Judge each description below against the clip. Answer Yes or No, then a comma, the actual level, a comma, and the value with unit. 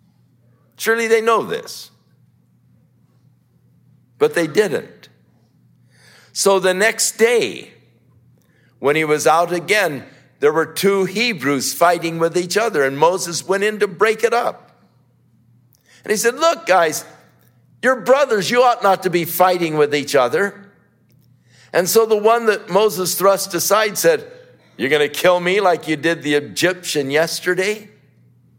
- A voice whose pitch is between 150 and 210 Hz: Yes, medium, 185 Hz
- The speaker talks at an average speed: Yes, average, 145 wpm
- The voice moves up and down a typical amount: No, wide, 6.5 semitones